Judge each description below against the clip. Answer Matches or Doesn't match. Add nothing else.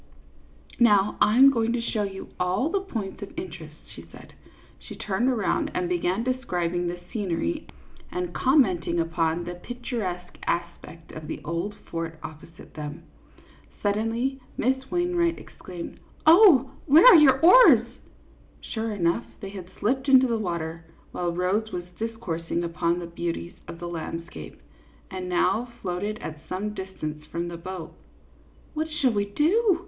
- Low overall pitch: Doesn't match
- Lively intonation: Matches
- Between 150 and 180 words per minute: Matches